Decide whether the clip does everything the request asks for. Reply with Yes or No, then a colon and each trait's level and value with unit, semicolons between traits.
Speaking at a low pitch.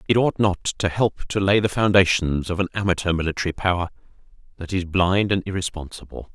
Yes: very low, 90 Hz